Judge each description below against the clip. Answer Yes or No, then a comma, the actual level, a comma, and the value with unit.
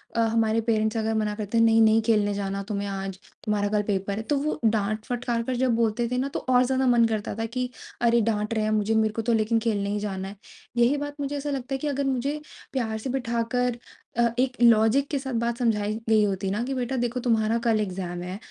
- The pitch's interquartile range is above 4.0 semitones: No, average, 2.8 semitones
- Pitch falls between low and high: No, high, 225 Hz